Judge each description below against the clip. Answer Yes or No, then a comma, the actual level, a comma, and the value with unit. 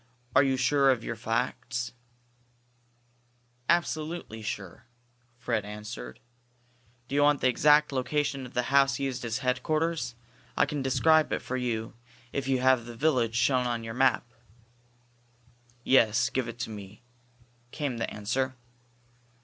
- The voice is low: Yes, low, 125 Hz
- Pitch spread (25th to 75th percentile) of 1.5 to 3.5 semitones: Yes, average, 2.9 semitones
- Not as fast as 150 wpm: Yes, average, 140 wpm